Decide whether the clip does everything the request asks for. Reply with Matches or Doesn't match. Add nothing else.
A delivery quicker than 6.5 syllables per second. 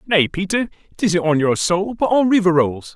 Doesn't match